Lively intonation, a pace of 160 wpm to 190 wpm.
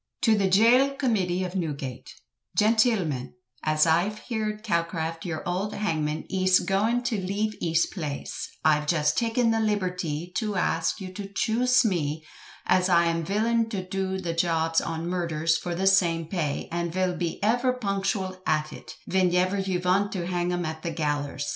No: average, 4.0 semitones; average, 175 wpm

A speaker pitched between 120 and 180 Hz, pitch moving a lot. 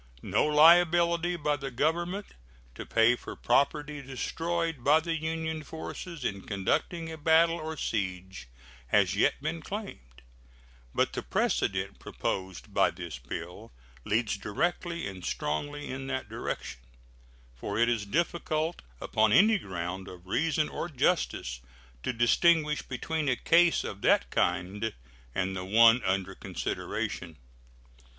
Yes: medium, 140 Hz; wide, 8.8 semitones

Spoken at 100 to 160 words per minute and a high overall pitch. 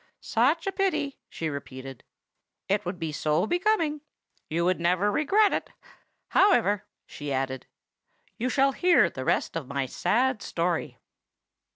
Yes: average, 140 wpm; high, 195 Hz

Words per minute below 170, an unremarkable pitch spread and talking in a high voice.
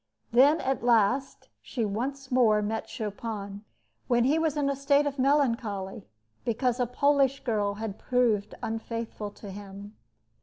Yes: average, 145 wpm; average, 4.5 semitones; high, 235 Hz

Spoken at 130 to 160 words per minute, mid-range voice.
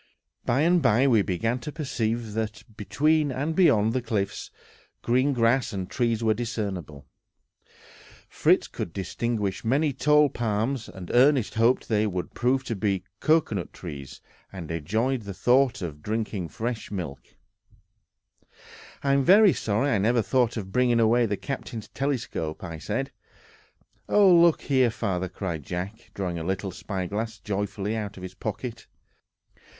No: average, 150 wpm; low, 110 Hz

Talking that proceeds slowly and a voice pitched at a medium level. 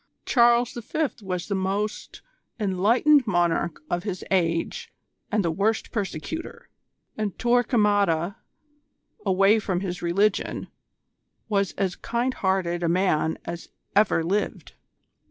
No: slow, 115 wpm; high, 195 Hz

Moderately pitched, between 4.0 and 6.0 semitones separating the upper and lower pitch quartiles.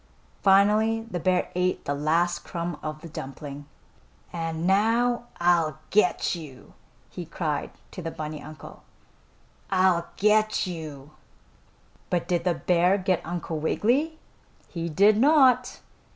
Yes: medium, 175 Hz; average, 4.6 semitones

